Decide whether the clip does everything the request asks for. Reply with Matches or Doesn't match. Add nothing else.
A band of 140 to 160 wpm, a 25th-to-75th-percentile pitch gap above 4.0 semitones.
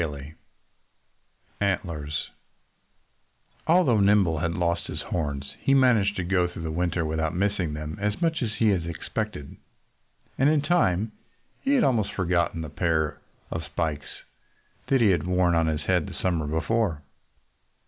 Matches